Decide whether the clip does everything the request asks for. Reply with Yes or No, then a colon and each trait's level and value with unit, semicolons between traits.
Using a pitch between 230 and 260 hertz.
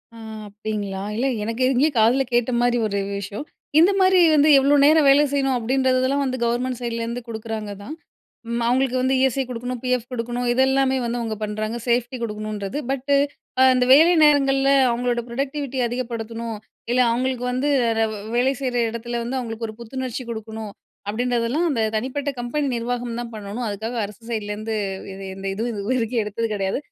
Yes: high, 240 Hz